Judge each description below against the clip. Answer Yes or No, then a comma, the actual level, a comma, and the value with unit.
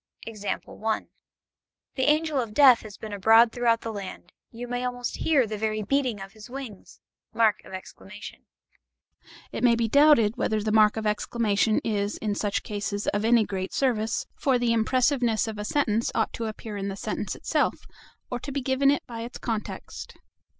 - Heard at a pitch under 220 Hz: No, high, 225 Hz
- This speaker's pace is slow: No, average, 170 wpm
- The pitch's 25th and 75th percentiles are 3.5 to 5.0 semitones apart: No, average, 2.8 semitones